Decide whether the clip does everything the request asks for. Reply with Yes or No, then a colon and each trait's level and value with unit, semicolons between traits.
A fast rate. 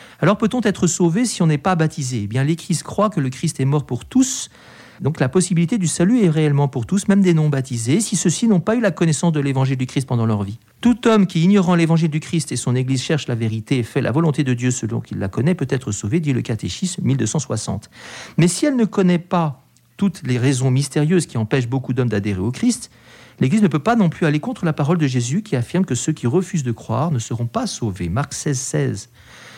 Yes: fast, 245 wpm